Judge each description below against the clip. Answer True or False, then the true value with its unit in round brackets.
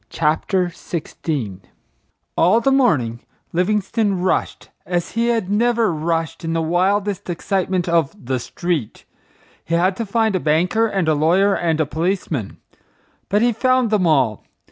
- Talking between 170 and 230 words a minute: False (145 wpm)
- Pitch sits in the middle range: True (180 Hz)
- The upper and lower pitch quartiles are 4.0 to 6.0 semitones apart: True (4.4 semitones)